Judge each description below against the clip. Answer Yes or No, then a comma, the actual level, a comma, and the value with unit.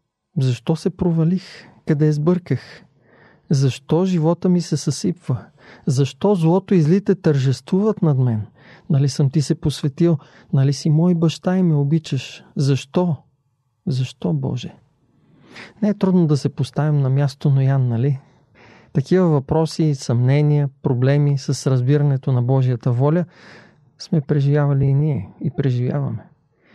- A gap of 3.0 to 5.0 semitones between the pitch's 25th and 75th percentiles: Yes, average, 3.6 semitones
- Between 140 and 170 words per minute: No, average, 130 wpm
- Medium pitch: Yes, medium, 145 Hz